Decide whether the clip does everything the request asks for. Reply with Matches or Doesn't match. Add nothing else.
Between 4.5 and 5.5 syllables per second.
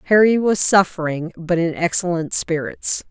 Matches